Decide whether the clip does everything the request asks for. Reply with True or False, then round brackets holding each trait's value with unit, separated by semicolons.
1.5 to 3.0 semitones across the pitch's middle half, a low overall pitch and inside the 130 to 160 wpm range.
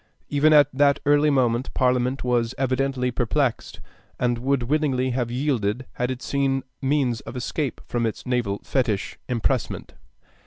True (2.4 semitones; 130 Hz; 145 wpm)